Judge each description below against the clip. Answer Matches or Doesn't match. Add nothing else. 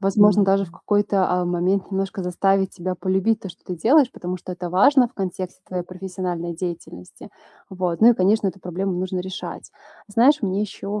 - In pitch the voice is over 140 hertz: Matches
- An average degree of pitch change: Doesn't match